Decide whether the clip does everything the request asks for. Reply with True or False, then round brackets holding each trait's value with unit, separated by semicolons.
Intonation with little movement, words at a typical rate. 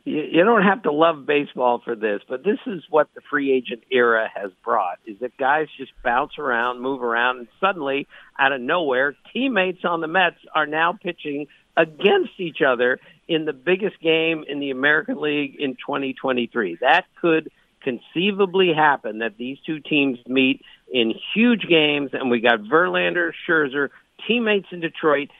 False (4.9 semitones; 170 wpm)